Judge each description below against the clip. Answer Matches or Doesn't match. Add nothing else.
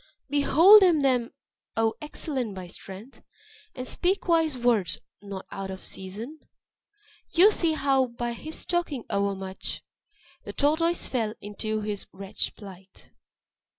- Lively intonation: Matches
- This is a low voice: Doesn't match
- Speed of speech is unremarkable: Doesn't match